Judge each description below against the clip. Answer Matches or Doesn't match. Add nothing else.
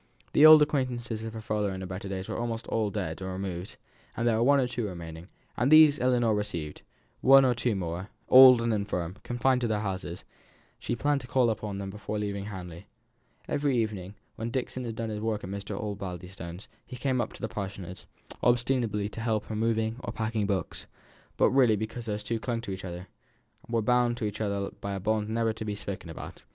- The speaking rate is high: Matches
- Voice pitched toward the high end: Doesn't match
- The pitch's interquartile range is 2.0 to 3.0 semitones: Doesn't match